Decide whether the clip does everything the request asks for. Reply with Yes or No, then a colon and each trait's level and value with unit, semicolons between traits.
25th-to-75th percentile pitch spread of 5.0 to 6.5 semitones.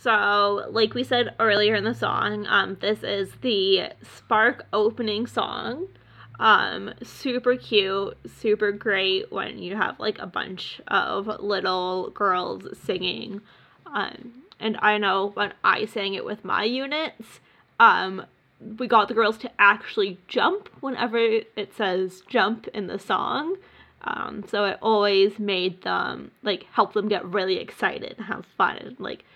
No: average, 3.0 semitones